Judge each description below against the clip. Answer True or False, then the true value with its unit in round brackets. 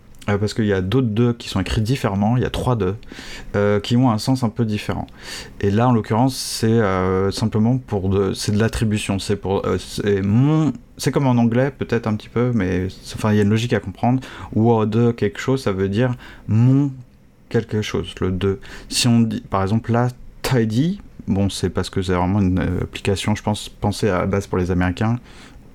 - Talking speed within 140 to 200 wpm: False (220 wpm)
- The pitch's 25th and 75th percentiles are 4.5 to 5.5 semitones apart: False (3.6 semitones)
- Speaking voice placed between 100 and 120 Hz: True (110 Hz)